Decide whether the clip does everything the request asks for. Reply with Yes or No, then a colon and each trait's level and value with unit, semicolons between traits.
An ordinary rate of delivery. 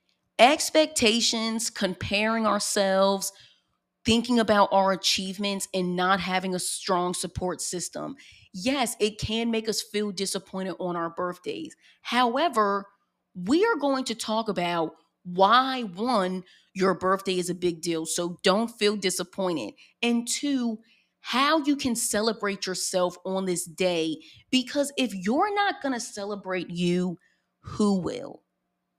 No: slow, 130 wpm